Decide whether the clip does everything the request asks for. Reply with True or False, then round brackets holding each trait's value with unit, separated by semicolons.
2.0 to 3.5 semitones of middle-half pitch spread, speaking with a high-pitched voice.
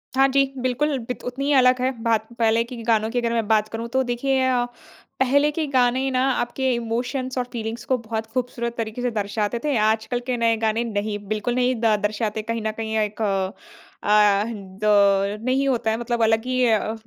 True (2.6 semitones; 235 Hz)